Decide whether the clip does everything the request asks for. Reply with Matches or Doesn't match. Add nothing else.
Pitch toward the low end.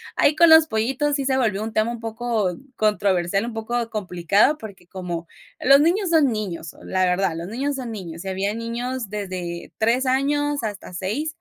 Doesn't match